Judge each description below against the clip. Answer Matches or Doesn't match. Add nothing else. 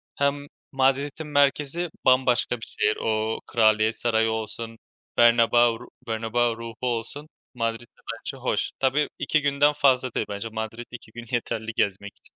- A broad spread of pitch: Doesn't match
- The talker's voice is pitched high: Doesn't match